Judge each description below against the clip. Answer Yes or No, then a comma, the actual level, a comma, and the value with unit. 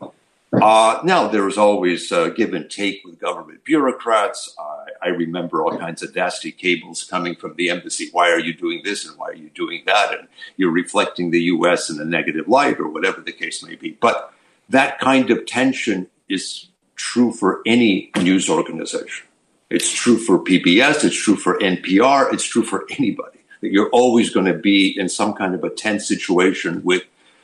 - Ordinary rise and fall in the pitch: No, wide, 5.8 semitones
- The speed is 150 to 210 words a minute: Yes, average, 190 wpm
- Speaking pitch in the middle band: No, low, 105 Hz